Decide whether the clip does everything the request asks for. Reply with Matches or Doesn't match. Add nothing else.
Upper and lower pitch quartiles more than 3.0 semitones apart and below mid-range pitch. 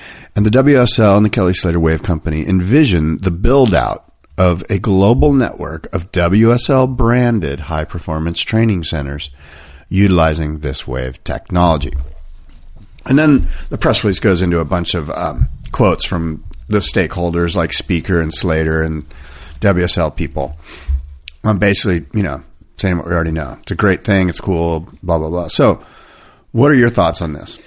Matches